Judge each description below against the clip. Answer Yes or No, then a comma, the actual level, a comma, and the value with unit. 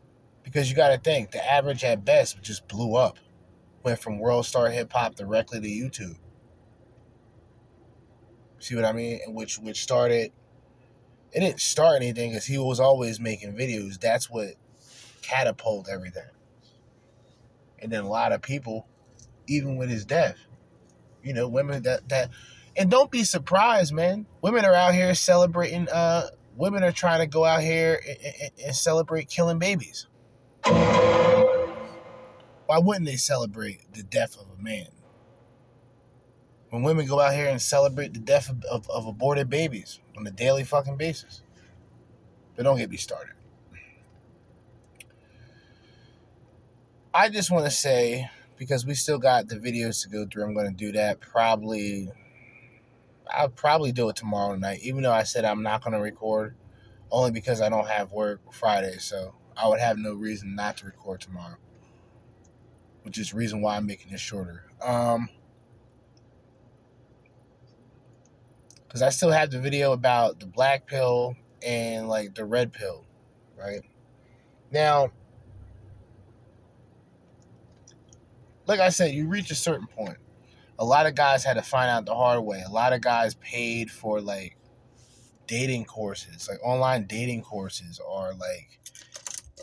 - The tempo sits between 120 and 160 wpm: Yes, average, 150 wpm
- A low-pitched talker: Yes, low, 120 Hz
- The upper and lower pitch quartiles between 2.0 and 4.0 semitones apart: Yes, average, 3.5 semitones